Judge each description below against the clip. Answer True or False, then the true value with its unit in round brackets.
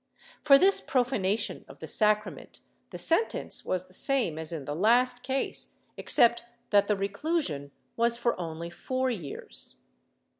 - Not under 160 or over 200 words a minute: False (145 wpm)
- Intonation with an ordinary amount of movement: False (6.4 semitones)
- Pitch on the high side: True (220 Hz)